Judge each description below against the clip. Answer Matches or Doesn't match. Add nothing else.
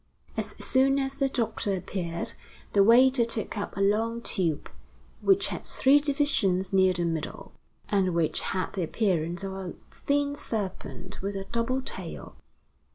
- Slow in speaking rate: Doesn't match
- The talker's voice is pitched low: Doesn't match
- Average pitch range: Doesn't match